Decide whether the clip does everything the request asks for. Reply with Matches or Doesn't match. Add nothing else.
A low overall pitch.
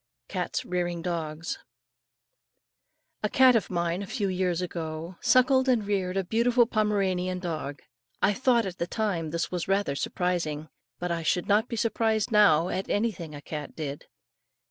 Doesn't match